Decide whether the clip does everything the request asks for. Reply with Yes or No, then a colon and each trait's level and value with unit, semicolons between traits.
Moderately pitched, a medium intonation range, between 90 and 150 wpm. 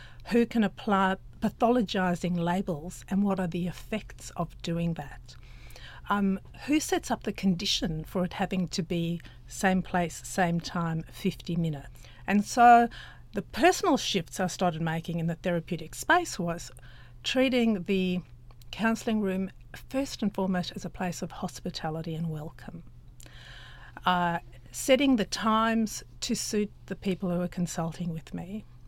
Yes: medium, 180 Hz; average, 3.9 semitones; average, 145 wpm